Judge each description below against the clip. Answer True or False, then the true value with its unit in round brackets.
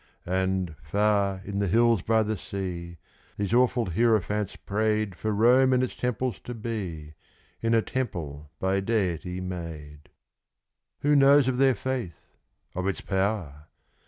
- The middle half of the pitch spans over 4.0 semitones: True (4.4 semitones)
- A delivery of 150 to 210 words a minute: False (140 wpm)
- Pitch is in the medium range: False (100 Hz)